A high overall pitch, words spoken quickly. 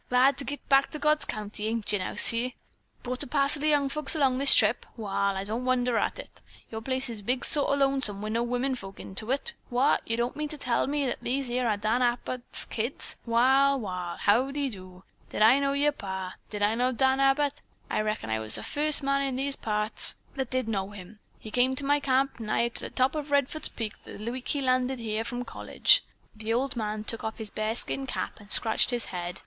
Yes: high, 245 Hz; fast, 230 wpm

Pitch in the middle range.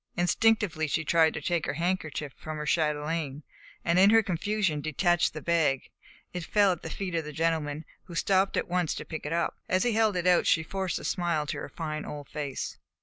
Yes: medium, 165 Hz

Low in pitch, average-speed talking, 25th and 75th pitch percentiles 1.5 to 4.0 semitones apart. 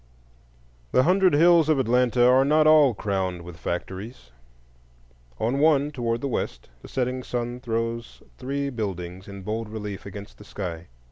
No: low, 120 Hz; average, 150 wpm; wide, 5.5 semitones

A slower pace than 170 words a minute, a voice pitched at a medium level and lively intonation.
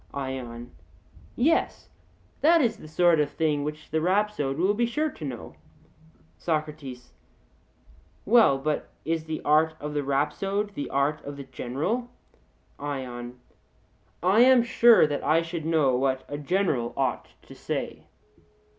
Yes: average, 140 wpm; medium, 155 Hz; wide, 6.0 semitones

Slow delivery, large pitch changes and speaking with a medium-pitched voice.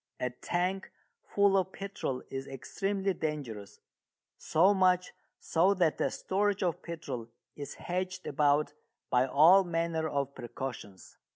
Yes: slow, 125 wpm; wide, 5.7 semitones; medium, 165 Hz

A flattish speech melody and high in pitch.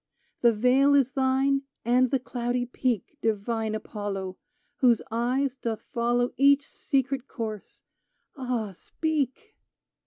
No: average, 3.1 semitones; very high, 250 Hz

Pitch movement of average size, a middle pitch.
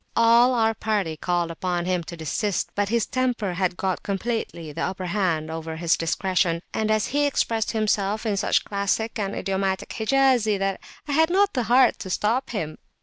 No: average, 4.3 semitones; high, 200 Hz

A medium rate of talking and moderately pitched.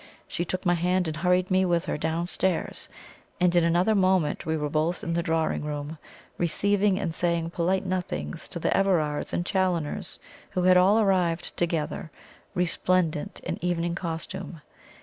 Yes: average, 160 wpm; medium, 175 Hz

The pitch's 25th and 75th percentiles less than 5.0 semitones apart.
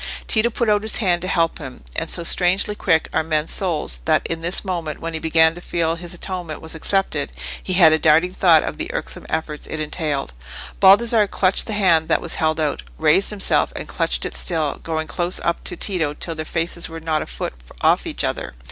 Yes: average, 2.7 semitones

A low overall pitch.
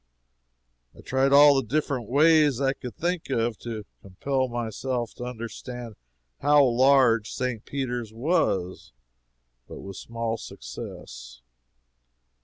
Yes: low, 125 Hz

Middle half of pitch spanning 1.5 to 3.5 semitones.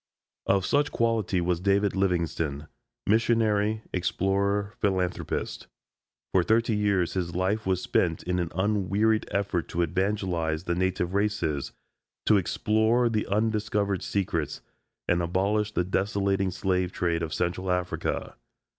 Yes: average, 2.9 semitones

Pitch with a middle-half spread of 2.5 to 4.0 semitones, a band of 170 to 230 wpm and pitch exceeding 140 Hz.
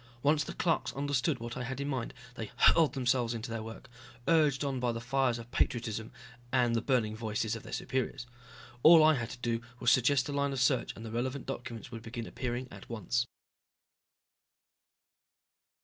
No: average, 2.8 semitones; average, 185 wpm; low, 125 Hz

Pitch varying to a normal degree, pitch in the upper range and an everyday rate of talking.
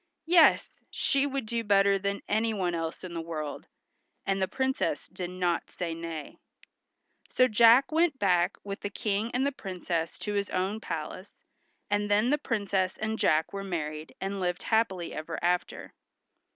Yes: average, 4.1 semitones; high, 195 Hz; average, 165 wpm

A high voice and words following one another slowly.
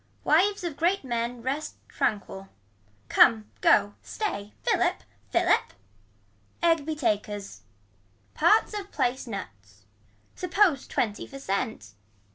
Yes: high, 245 Hz; slow, 105 wpm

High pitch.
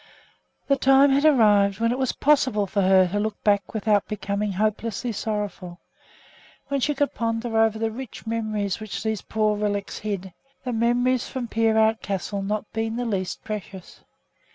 Yes: high, 220 Hz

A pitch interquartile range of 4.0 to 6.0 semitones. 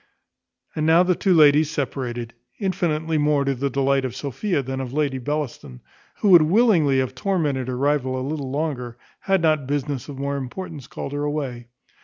No: average, 3.1 semitones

